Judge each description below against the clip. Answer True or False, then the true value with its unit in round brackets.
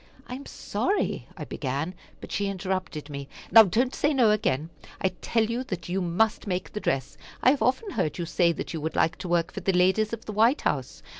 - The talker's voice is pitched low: False (190 Hz)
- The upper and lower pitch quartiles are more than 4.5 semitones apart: True (5.0 semitones)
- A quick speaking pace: True (225 wpm)